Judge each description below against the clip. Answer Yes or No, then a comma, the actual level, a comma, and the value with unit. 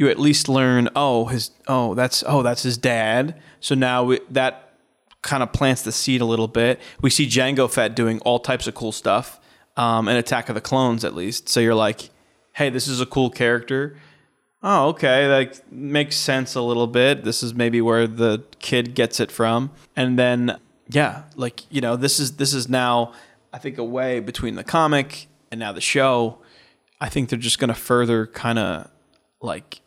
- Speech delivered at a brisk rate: No, average, 195 wpm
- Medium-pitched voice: No, low, 125 Hz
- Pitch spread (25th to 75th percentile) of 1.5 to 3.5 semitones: Yes, narrow, 2.6 semitones